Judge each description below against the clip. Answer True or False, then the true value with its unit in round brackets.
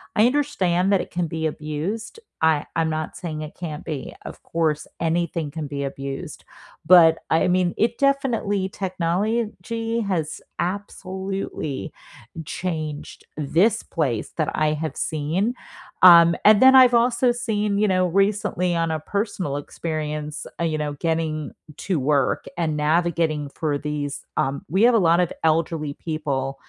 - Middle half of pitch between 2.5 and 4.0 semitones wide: False (4.5 semitones)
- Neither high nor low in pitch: True (165 Hz)